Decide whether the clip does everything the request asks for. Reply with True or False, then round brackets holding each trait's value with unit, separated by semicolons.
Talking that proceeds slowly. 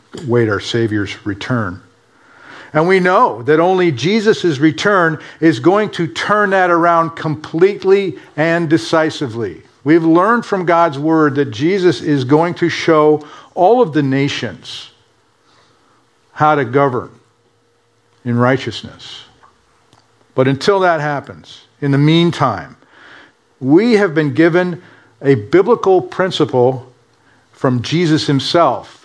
True (120 wpm)